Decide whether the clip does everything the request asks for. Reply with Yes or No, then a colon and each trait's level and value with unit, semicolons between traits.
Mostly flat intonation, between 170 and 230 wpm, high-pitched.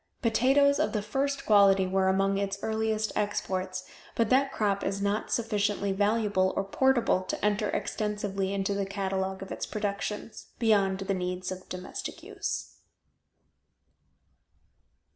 No: narrow, 2.1 semitones; slow, 135 wpm; high, 200 Hz